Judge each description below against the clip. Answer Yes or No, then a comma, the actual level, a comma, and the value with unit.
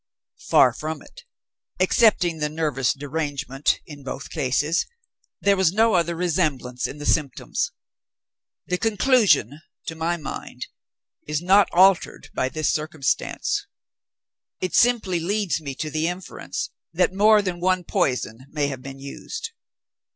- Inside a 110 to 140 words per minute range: Yes, slow, 135 wpm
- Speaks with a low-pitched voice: No, medium, 160 Hz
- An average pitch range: Yes, average, 4.5 semitones